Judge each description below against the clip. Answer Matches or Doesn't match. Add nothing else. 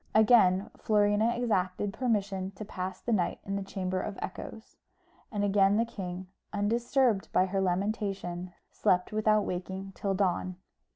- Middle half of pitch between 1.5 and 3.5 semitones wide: Matches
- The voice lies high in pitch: Matches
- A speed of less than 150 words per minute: Matches